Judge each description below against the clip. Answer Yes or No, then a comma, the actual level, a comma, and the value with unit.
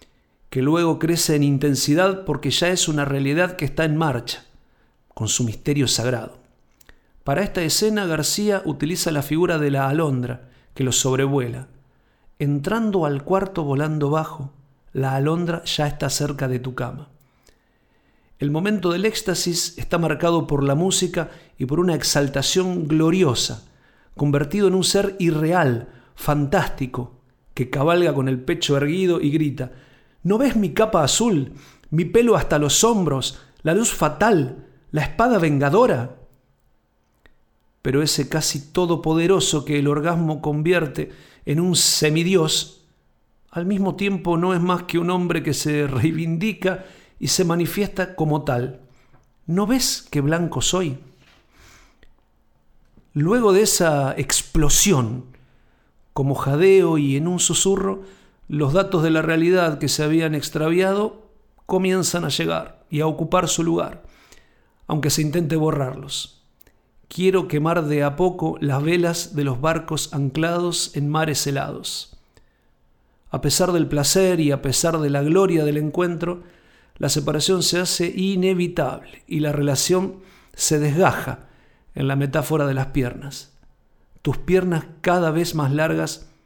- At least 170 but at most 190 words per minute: No, average, 140 wpm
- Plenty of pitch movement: No, average, 4.1 semitones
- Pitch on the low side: No, medium, 155 Hz